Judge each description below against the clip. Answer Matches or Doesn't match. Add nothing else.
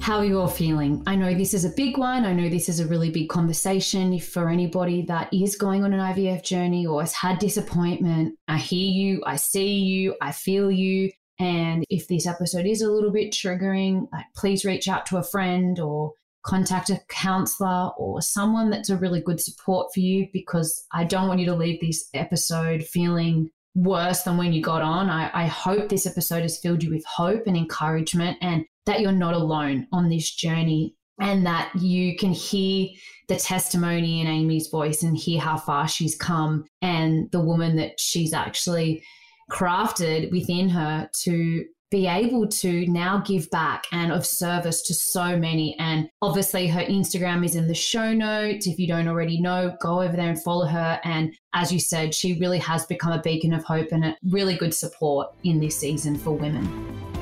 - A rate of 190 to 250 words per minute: Matches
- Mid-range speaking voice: Matches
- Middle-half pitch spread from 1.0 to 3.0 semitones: Matches